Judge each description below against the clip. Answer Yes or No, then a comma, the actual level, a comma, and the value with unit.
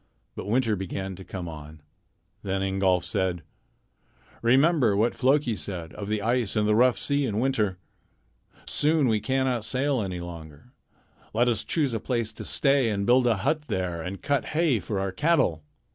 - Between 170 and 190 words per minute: Yes, average, 175 wpm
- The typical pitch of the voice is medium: No, low, 110 Hz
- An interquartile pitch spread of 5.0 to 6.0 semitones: Yes, wide, 5.5 semitones